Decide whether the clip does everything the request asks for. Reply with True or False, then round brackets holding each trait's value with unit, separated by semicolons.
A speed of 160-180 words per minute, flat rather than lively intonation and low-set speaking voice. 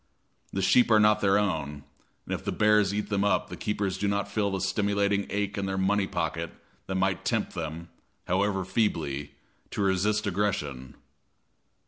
True (170 wpm; 1.8 semitones; 100 Hz)